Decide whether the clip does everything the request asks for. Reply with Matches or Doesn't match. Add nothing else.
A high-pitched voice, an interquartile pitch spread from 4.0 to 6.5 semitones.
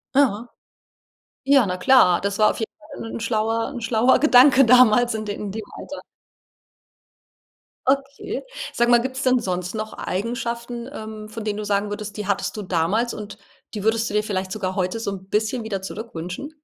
Doesn't match